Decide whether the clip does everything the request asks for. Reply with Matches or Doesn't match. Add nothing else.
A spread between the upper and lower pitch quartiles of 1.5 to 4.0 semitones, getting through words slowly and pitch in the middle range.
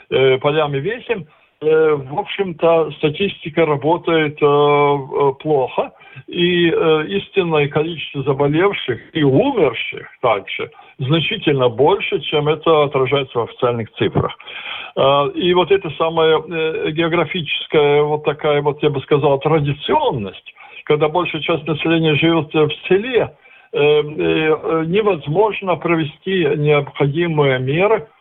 Matches